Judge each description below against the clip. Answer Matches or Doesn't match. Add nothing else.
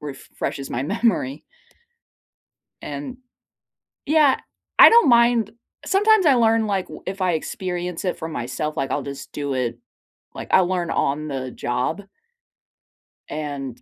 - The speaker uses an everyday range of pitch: Doesn't match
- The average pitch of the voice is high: Doesn't match